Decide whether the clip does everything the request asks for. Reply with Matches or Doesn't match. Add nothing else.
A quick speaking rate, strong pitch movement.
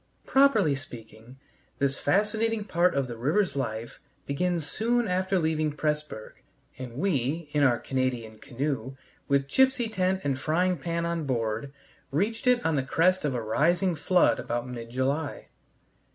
Doesn't match